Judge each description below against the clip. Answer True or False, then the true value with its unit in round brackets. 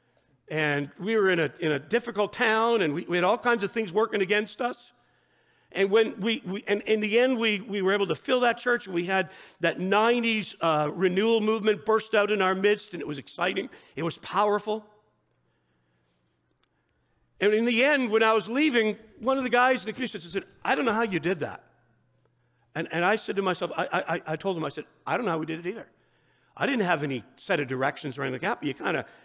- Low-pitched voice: False (205 Hz)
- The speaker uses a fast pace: True (235 wpm)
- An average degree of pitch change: True (5.0 semitones)